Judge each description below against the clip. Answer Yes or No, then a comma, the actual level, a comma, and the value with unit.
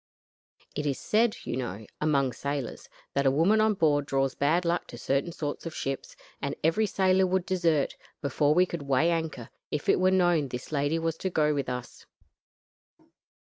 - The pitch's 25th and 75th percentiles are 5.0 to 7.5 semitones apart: No, average, 4.1 semitones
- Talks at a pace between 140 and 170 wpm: No, average, 185 wpm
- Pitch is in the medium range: Yes, medium, 150 Hz